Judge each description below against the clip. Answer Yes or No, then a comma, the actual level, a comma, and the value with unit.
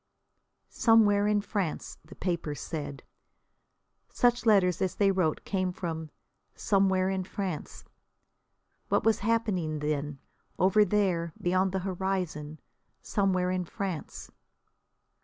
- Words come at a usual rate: No, slow, 110 wpm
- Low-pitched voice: No, medium, 185 Hz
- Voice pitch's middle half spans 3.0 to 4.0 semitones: Yes, average, 3.4 semitones